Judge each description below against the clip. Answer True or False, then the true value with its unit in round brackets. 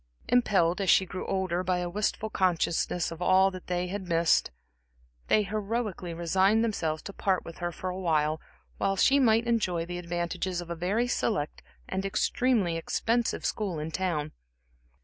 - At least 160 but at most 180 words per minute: True (170 wpm)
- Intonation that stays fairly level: False (3.3 semitones)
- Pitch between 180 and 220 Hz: True (185 Hz)